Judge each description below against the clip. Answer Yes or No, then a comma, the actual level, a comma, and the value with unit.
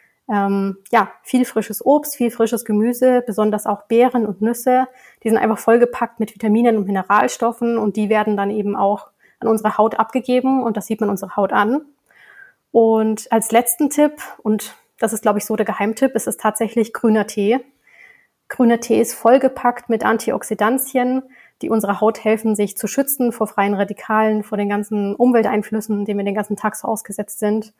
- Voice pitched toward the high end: Yes, high, 220 Hz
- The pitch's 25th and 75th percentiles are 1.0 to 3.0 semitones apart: Yes, narrow, 2.5 semitones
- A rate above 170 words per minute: Yes, average, 180 wpm